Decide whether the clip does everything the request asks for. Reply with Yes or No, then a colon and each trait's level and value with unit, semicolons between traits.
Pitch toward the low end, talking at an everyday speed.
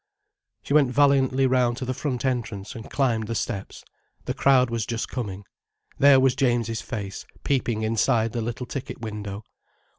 Yes: low, 120 Hz; average, 160 wpm